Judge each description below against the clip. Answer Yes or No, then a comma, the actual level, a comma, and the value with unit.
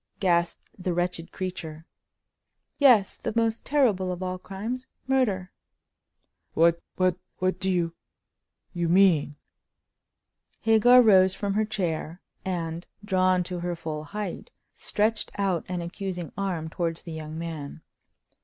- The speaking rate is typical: No, slow, 110 wpm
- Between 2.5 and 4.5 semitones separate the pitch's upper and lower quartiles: Yes, average, 2.9 semitones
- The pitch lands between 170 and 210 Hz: Yes, medium, 185 Hz